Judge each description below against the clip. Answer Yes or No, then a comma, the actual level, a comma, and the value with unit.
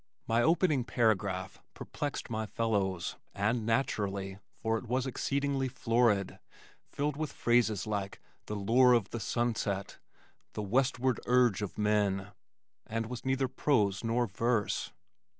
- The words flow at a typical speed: No, slow, 130 wpm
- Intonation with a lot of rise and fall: No, average, 3.7 semitones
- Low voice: Yes, low, 115 Hz